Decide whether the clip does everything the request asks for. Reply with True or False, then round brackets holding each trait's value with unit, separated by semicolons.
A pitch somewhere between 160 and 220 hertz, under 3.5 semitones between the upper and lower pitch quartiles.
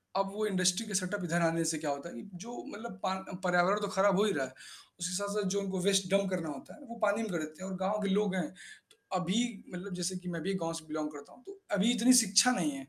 True (190 Hz; 3.0 semitones)